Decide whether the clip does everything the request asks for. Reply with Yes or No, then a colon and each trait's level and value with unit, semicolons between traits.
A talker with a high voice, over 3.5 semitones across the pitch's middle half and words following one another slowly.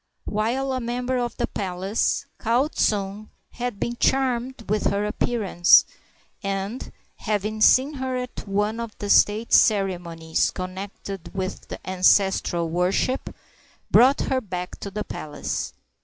Yes: high, 210 Hz; average, 4.0 semitones; slow, 130 wpm